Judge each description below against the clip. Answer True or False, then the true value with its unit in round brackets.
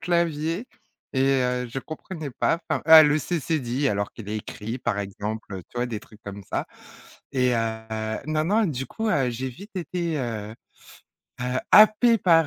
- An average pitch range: False (6.6 semitones)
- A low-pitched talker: True (130 Hz)